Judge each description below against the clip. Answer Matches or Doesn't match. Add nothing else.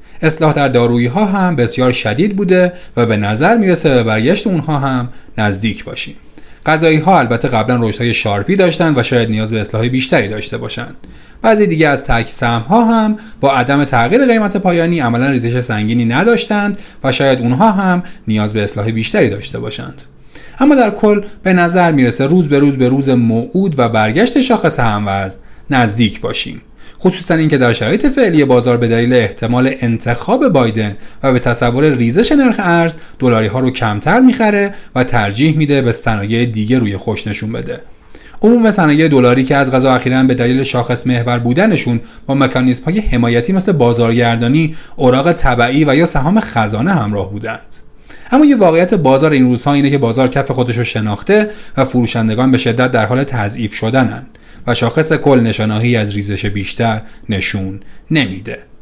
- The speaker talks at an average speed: Doesn't match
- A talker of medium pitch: Doesn't match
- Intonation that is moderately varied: Doesn't match